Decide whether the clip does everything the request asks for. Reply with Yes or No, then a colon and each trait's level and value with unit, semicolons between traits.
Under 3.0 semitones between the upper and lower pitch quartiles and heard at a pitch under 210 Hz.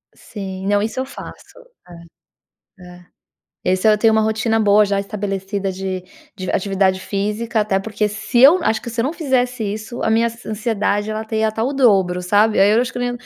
No: narrow, 2.6 semitones; high, 215 Hz